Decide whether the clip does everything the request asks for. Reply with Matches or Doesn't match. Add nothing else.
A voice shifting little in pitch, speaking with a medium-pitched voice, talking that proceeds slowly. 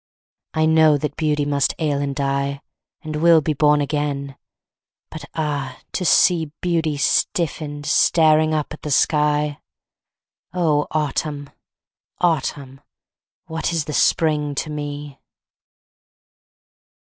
Matches